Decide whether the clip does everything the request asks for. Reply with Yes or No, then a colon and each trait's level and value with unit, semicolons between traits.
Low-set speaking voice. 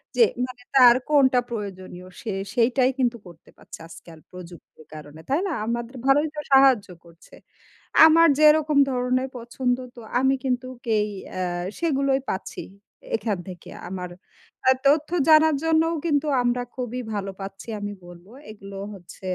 No: high, 245 Hz